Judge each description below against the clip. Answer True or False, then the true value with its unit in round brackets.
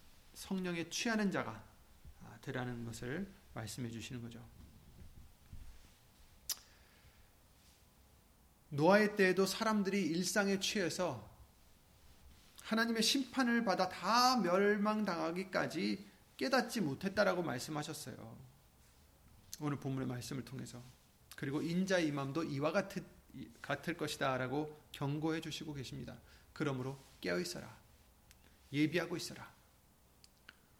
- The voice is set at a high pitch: False (145 Hz)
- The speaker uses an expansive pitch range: True (8.3 semitones)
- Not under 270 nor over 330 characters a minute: False (240 characters per minute)